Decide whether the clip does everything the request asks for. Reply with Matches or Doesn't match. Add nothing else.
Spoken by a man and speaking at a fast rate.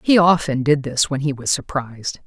Doesn't match